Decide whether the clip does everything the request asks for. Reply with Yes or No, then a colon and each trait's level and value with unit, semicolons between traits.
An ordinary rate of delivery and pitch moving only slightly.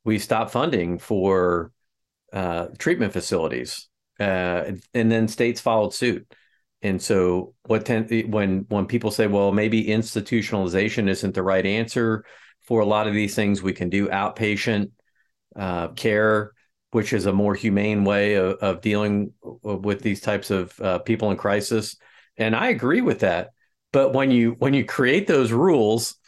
Yes: average, 160 wpm; narrow, 2.3 semitones